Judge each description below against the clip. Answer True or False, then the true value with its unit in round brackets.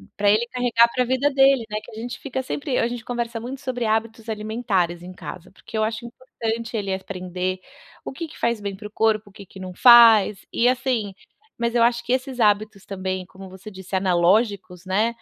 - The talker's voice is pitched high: True (220 Hz)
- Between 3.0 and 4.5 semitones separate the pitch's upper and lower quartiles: True (3.7 semitones)